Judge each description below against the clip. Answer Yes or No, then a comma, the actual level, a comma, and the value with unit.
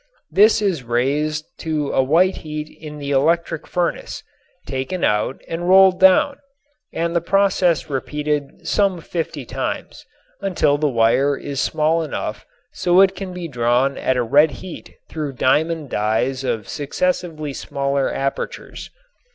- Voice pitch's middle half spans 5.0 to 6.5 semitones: No, average, 4.3 semitones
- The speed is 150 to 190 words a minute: No, average, 140 wpm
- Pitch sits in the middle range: Yes, medium, 150 Hz